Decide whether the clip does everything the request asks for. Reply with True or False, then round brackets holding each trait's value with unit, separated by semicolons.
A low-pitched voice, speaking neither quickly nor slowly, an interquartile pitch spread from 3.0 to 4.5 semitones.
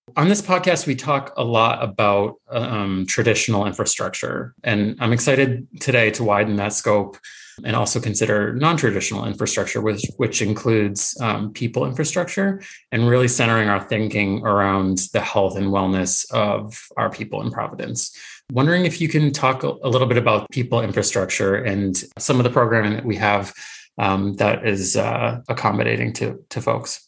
True (115 Hz; 165 wpm; 3.8 semitones)